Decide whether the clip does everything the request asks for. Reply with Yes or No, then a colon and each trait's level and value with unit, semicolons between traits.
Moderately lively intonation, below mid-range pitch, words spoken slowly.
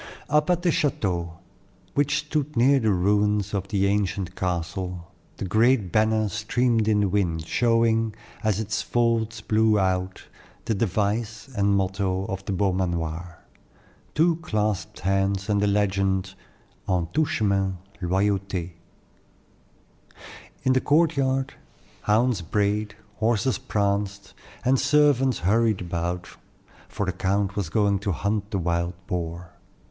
Yes: average, 3.4 semitones; low, 100 Hz; slow, 130 wpm